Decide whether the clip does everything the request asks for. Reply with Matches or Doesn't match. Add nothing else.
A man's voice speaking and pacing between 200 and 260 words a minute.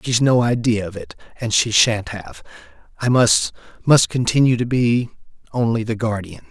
Doesn't match